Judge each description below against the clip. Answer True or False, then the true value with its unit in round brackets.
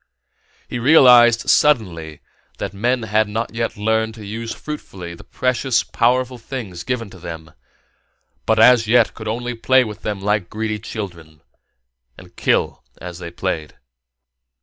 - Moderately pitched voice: False (110 Hz)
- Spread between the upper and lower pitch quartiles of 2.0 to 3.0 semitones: False (4.0 semitones)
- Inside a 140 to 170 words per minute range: True (145 wpm)